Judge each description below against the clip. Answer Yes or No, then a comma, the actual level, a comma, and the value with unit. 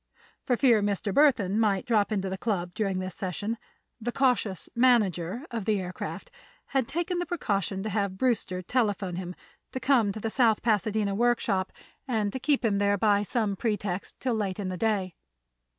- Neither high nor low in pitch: No, high, 210 Hz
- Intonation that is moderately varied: Yes, average, 3.6 semitones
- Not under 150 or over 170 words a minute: No, average, 180 wpm